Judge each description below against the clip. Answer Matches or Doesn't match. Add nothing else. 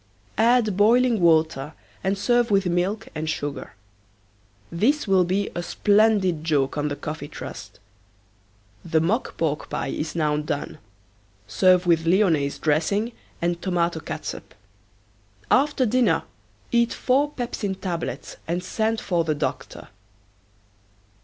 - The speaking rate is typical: Doesn't match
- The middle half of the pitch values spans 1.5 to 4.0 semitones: Doesn't match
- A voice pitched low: Doesn't match